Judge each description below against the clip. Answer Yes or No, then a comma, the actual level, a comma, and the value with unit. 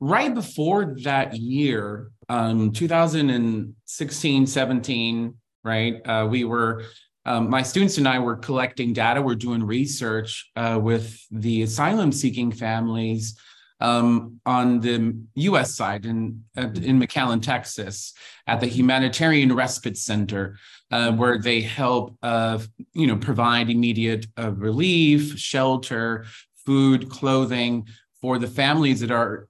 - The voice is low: Yes, low, 120 Hz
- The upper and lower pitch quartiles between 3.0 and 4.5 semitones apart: No, narrow, 2.6 semitones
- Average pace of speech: No, slow, 120 wpm